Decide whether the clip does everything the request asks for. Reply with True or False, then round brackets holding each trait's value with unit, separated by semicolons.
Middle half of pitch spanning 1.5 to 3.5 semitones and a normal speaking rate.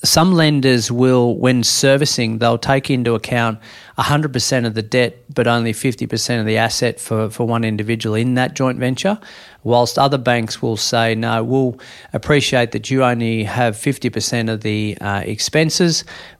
True (2.8 semitones; 160 wpm)